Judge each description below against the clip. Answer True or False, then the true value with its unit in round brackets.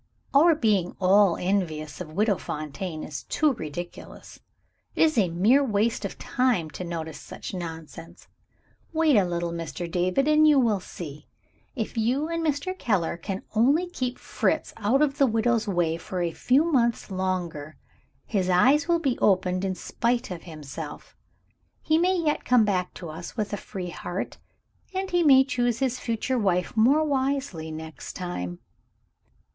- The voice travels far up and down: True (7.4 semitones)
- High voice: True (205 Hz)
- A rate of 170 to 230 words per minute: False (160 wpm)